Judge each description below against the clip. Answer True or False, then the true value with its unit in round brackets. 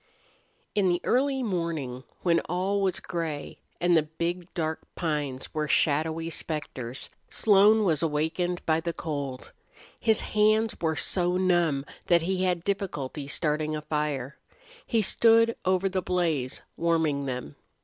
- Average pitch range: True (3.7 semitones)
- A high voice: False (165 Hz)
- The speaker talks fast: False (140 wpm)